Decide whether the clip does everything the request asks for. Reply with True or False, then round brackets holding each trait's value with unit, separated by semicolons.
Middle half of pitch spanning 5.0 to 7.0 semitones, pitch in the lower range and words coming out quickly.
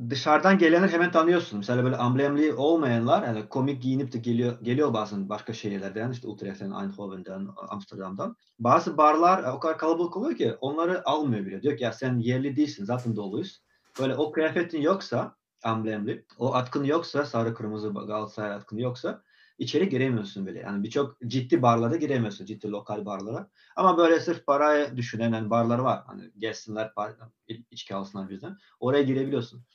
True (5.4 semitones; 120 Hz; 160 wpm)